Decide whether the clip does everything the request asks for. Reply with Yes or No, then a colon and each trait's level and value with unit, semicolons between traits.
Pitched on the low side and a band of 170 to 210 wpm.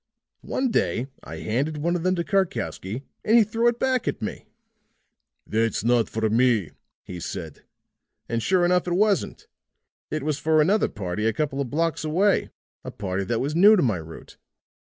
No: medium, 150 Hz; average, 180 wpm